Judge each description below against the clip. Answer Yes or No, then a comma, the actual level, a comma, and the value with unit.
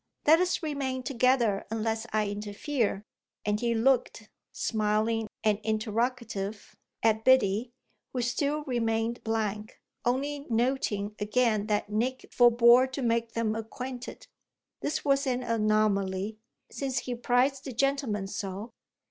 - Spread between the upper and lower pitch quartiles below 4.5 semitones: Yes, average, 3.2 semitones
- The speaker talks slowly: Yes, slow, 120 wpm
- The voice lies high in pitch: Yes, high, 230 Hz